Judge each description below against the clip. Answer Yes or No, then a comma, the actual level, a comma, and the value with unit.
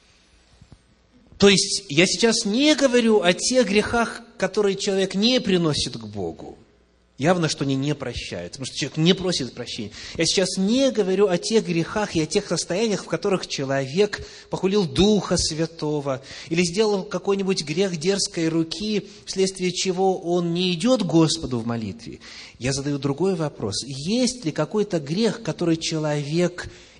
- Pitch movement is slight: No, average, 5.2 semitones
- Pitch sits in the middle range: Yes, medium, 180 Hz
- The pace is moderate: Yes, average, 150 wpm